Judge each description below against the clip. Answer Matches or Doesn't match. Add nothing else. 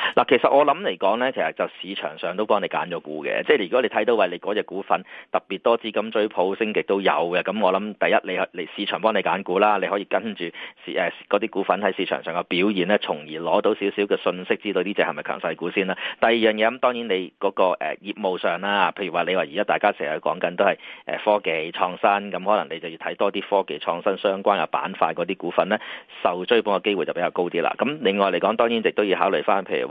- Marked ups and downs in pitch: Doesn't match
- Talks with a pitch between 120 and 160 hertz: Doesn't match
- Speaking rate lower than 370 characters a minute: Doesn't match